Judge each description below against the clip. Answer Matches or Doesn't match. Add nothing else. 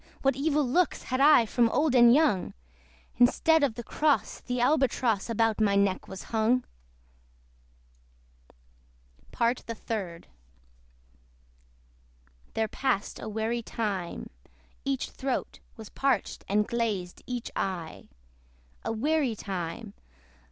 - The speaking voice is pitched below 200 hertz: Doesn't match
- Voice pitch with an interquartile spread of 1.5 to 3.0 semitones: Doesn't match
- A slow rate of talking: Matches